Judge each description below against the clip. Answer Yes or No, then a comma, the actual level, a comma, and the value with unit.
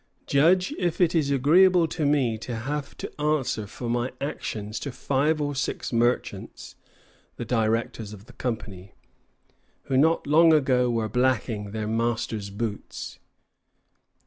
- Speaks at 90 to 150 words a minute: Yes, average, 140 wpm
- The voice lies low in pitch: Yes, low, 125 Hz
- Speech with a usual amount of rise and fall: Yes, average, 4.9 semitones